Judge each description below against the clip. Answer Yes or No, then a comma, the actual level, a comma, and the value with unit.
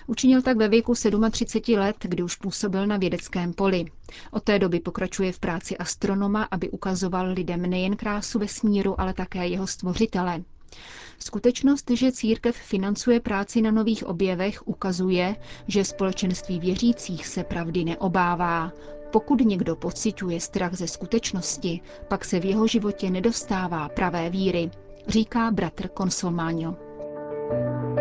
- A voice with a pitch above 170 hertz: Yes, high, 190 Hz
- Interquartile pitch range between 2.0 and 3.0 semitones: No, average, 3.4 semitones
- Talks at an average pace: Yes, average, 130 wpm